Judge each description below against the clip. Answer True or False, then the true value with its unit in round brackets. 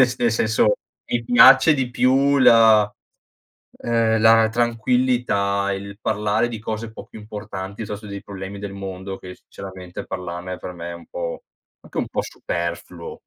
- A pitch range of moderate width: True (3.4 semitones)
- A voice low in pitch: True (105 Hz)